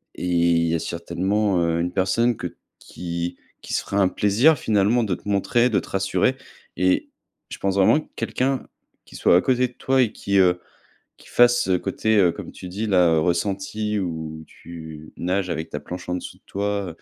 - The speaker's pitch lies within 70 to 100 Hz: Yes, very low, 95 Hz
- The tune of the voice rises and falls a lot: No, average, 3.6 semitones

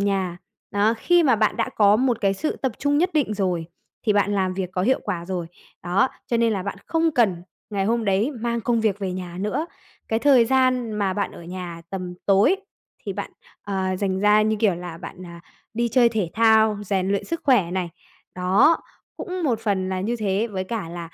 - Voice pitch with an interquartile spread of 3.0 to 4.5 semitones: Yes, average, 3.8 semitones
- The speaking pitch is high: Yes, high, 205 Hz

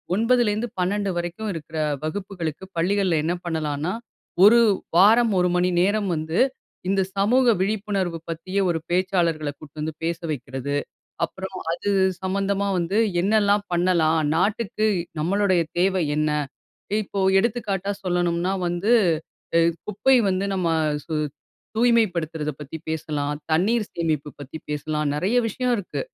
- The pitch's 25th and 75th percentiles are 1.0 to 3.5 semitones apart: No, average, 3.9 semitones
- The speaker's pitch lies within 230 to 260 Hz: No, medium, 185 Hz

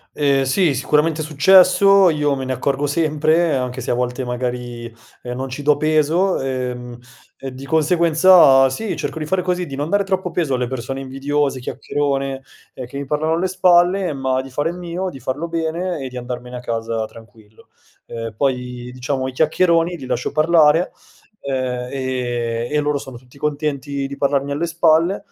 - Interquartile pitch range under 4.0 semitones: No, average, 4.3 semitones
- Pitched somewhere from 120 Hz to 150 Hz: Yes, medium, 140 Hz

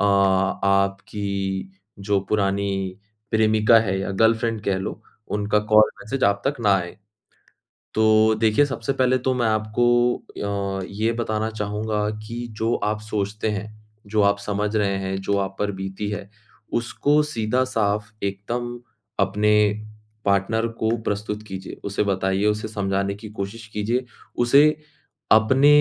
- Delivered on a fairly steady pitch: Yes, narrow, 2.1 semitones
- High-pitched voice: No, low, 105 Hz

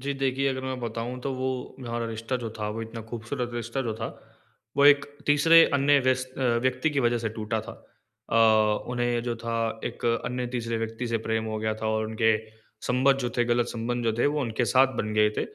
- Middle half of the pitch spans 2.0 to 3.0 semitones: Yes, narrow, 2.6 semitones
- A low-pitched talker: Yes, low, 120 Hz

